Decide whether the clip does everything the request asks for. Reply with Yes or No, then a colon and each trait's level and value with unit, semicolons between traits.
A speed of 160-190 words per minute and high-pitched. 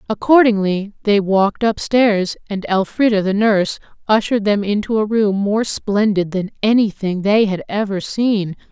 No: average, 145 wpm; high, 205 Hz